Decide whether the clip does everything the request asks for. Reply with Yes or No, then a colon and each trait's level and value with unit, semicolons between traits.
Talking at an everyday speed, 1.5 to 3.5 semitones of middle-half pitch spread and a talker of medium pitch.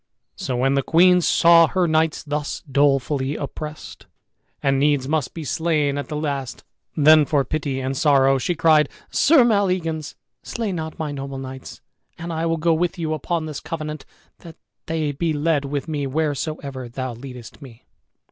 Yes: average, 165 wpm; average, 3.0 semitones; medium, 150 Hz